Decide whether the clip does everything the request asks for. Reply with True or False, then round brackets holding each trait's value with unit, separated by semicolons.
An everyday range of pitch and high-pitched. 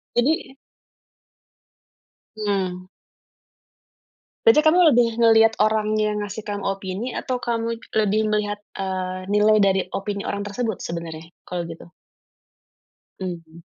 True (3.0 semitones; 205 Hz)